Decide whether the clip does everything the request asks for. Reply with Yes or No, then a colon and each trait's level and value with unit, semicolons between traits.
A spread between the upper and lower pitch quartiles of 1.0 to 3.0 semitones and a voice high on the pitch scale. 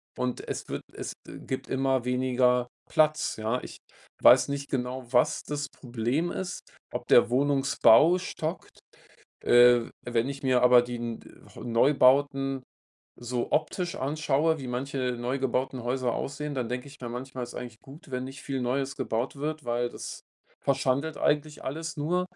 No: narrow, 2.5 semitones; low, 130 Hz